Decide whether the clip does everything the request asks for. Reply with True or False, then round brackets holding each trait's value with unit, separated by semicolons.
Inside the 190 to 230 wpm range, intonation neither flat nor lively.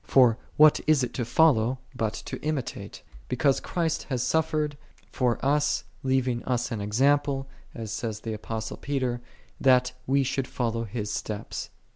False (165 wpm; 3.5 semitones)